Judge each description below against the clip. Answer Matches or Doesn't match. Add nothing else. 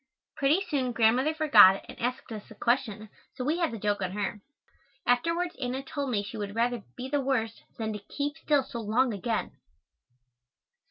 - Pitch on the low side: Doesn't match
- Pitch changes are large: Doesn't match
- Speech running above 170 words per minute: Matches